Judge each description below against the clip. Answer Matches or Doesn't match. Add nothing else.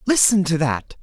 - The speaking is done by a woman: Doesn't match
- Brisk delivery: Doesn't match